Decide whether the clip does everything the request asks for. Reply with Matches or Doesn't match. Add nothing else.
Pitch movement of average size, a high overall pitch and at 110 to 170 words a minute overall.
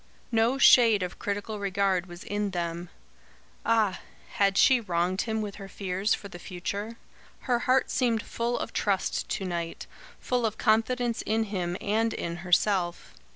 Matches